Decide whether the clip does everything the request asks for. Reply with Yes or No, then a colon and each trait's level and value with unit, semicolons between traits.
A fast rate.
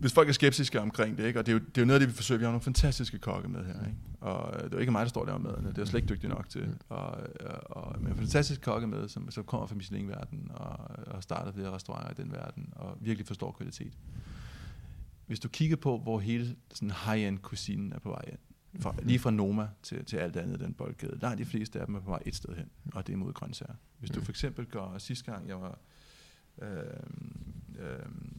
Yes: fast, 250 wpm